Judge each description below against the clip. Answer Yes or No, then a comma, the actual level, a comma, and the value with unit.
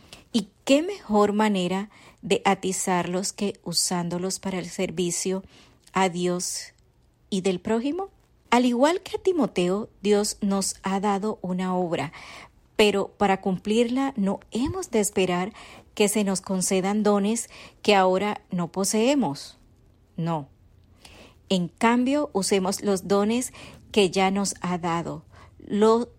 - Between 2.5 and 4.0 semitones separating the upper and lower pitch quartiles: Yes, average, 2.8 semitones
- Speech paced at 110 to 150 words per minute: Yes, slow, 125 wpm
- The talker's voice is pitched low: No, high, 195 Hz